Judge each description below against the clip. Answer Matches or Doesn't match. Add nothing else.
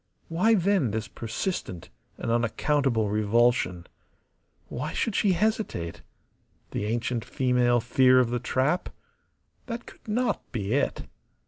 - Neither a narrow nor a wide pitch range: Doesn't match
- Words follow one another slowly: Matches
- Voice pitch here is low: Matches